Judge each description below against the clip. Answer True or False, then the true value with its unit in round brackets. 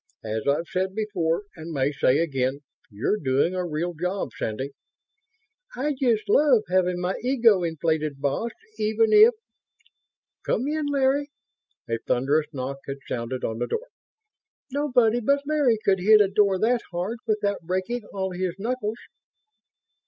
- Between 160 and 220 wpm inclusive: False (145 wpm)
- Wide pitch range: True (7.5 semitones)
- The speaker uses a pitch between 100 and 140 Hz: False (190 Hz)